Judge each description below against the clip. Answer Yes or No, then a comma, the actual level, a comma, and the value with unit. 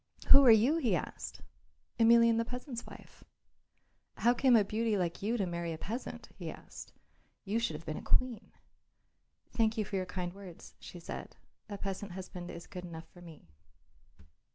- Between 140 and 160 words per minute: No, average, 175 wpm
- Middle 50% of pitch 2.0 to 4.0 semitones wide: No, average, 4.8 semitones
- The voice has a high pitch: Yes, high, 200 Hz